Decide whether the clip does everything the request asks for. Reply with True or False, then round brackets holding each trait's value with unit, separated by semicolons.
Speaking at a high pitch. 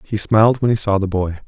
False (105 Hz)